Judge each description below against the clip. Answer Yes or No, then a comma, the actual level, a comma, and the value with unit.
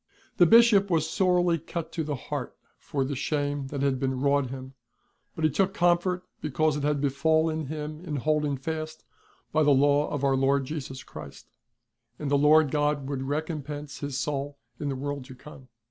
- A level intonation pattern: Yes, narrow, 2.2 semitones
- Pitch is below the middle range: No, medium, 150 Hz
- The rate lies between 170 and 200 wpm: Yes, average, 185 wpm